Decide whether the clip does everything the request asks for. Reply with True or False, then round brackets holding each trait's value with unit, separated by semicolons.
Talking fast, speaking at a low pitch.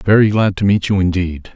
True (230 wpm; 95 Hz)